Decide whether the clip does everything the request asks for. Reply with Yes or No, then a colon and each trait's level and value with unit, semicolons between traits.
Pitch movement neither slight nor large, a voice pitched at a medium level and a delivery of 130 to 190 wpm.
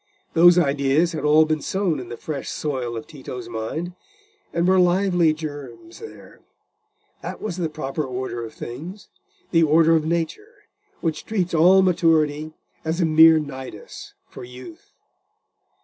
Yes: average, 3.9 semitones; medium, 160 Hz; average, 145 wpm